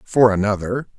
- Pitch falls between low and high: No, low, 110 Hz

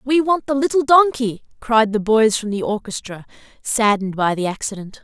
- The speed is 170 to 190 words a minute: Yes, average, 180 wpm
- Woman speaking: Yes, female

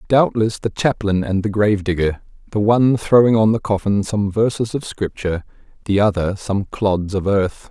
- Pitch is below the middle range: Yes, low, 105 Hz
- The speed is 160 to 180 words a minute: Yes, average, 165 wpm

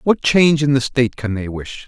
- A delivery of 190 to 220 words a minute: No, fast, 255 wpm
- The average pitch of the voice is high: No, low, 130 Hz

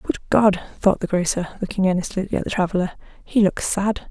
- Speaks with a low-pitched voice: No, high, 190 Hz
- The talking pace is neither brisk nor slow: Yes, average, 190 wpm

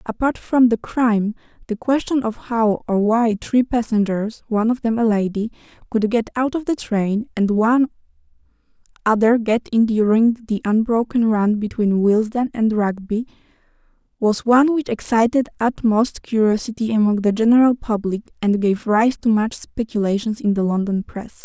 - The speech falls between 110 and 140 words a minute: No, average, 160 wpm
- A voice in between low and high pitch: No, high, 225 Hz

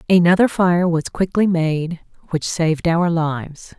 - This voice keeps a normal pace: Yes, average, 145 wpm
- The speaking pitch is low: No, medium, 170 Hz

